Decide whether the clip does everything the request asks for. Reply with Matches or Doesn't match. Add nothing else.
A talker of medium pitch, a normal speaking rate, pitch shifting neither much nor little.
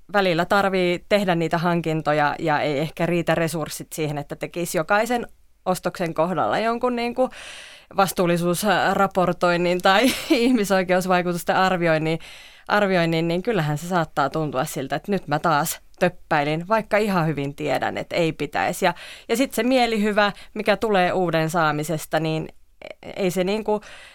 Matches